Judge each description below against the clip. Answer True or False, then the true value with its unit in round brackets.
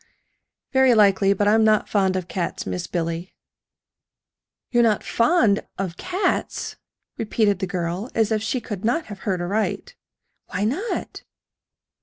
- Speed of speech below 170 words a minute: True (140 wpm)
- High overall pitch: True (205 Hz)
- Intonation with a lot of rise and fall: False (3.7 semitones)